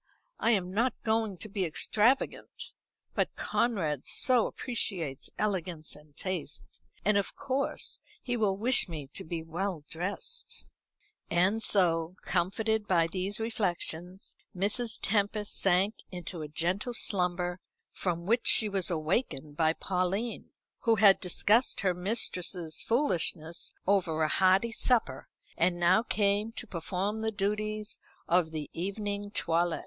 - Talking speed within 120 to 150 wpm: Yes, slow, 135 wpm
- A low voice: No, high, 190 Hz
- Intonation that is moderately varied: Yes, average, 3.8 semitones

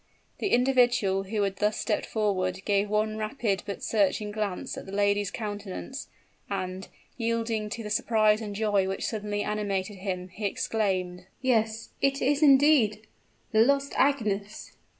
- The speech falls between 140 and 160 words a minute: Yes, average, 150 wpm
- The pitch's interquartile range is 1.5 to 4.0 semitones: Yes, narrow, 2.4 semitones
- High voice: Yes, high, 210 Hz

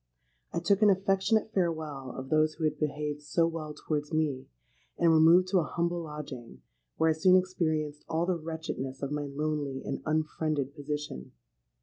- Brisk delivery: No, average, 165 wpm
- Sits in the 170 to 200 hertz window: No, medium, 155 Hz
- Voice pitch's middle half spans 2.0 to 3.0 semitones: Yes, narrow, 2.4 semitones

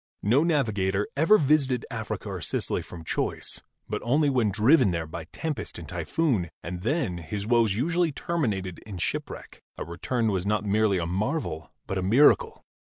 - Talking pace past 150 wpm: Yes, average, 170 wpm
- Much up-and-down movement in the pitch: Yes, wide, 7.1 semitones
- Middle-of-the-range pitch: No, low, 110 Hz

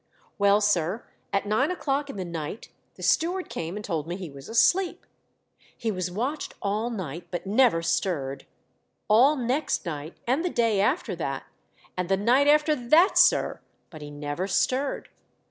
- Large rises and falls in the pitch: Yes, wide, 7.5 semitones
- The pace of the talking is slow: No, average, 165 wpm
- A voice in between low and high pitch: No, high, 205 Hz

